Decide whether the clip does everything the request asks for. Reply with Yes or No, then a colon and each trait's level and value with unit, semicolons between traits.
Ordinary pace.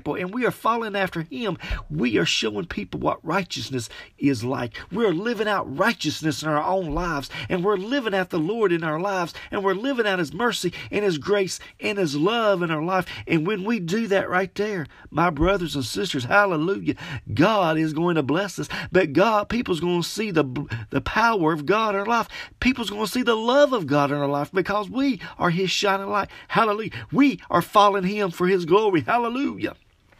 No: fast, 210 wpm